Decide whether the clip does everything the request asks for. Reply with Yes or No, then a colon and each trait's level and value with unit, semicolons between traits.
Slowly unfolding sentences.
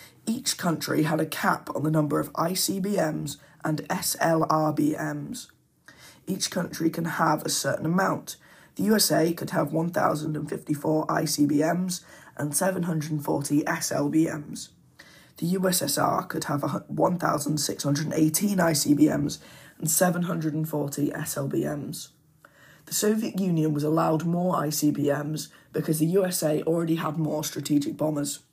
Yes: slow, 110 wpm